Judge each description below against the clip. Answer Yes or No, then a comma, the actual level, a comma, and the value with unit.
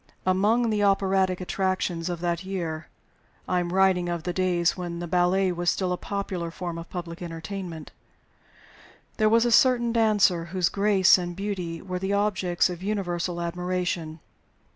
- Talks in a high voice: No, medium, 180 Hz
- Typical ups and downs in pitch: No, narrow, 2.1 semitones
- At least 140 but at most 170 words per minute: Yes, average, 160 wpm